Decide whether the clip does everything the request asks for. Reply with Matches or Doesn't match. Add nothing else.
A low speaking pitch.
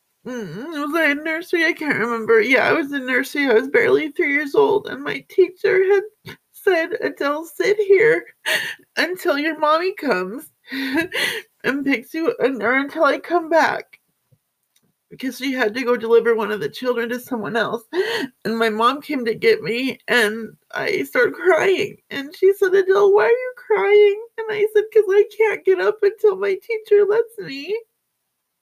Doesn't match